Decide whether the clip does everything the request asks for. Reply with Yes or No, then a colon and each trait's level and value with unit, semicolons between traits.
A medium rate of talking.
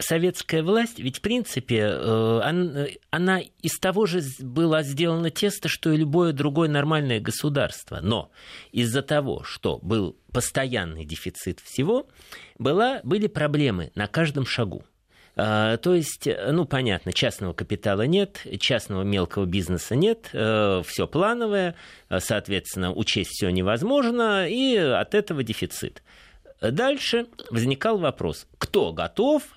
Yes: average, 120 wpm